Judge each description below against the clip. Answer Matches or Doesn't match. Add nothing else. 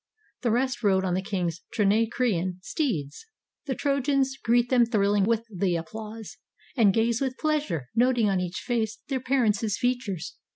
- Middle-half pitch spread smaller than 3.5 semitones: Doesn't match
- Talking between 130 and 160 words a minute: Matches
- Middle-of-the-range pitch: Doesn't match